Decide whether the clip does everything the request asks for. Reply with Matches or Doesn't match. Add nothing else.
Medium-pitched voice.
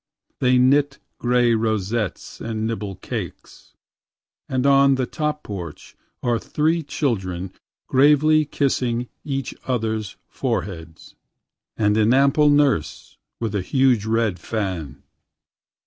Doesn't match